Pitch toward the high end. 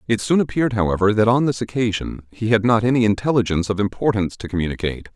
No: low, 110 Hz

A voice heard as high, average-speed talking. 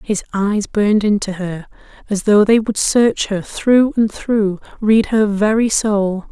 Yes: high, 210 Hz; average, 170 wpm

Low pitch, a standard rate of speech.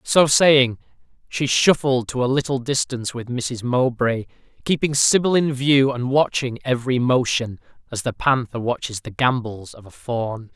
Yes: low, 125 Hz; average, 160 wpm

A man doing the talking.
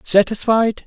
Yes: male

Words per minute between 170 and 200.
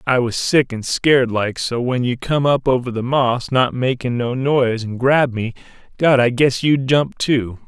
Yes: average, 195 wpm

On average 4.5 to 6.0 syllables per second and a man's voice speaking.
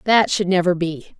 No: 4.8 syllables/s; female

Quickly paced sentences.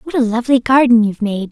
Yes: fast, 235 wpm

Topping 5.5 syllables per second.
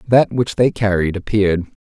No: 5.3 syllables/s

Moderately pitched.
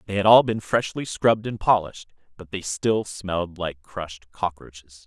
No: very low, 95 Hz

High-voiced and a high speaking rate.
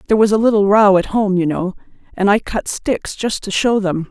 Yes: high, 205 Hz; fast, 250 wpm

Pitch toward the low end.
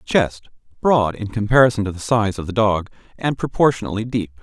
Yes: low, 110 Hz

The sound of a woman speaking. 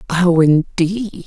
Yes: female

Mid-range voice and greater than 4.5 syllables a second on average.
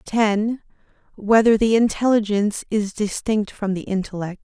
No: high, 210 Hz; 5.1 syllables/s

